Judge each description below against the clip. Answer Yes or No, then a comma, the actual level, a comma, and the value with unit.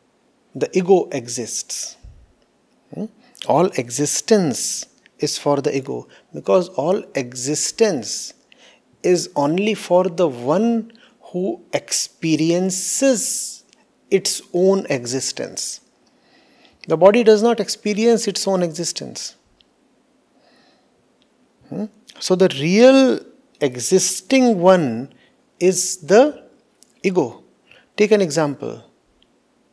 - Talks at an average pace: No, slow, 85 wpm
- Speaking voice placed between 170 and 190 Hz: Yes, medium, 185 Hz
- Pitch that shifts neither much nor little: No, wide, 6.1 semitones